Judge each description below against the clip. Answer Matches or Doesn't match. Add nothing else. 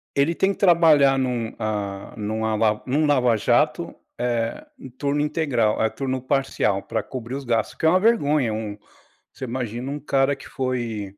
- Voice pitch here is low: Matches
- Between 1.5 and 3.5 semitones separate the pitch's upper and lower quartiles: Doesn't match